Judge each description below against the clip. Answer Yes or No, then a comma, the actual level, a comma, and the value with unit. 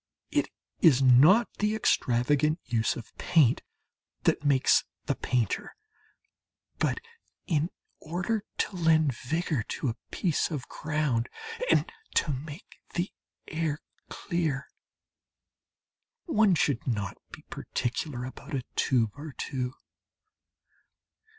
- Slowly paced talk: Yes, slow, 110 wpm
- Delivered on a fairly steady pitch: No, average, 4.7 semitones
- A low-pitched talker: No, medium, 145 Hz